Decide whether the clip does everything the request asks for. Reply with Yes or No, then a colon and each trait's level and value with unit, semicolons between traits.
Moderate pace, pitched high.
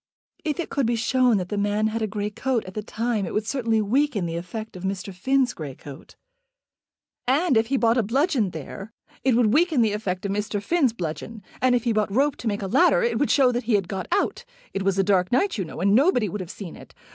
No: fast, 250 wpm; high, 220 Hz